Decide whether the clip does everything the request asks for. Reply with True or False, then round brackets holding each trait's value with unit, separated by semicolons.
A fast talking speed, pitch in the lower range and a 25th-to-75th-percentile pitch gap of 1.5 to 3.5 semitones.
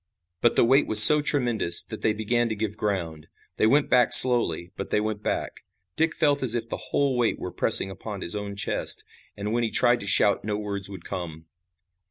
True (215 wpm; 110 Hz; 3.2 semitones)